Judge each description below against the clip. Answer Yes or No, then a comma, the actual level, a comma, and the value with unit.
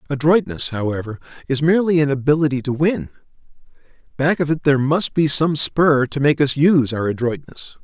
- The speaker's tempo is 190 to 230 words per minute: No, average, 170 wpm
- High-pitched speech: No, medium, 145 Hz